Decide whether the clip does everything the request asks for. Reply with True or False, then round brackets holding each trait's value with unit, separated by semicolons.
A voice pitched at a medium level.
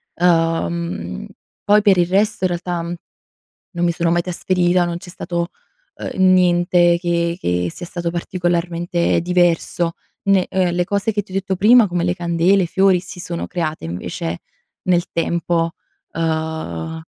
True (175 Hz)